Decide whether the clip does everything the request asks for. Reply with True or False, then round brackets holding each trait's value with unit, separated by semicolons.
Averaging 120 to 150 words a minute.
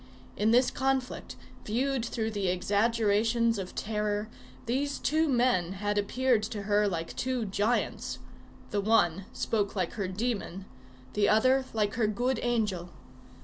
True (140 wpm)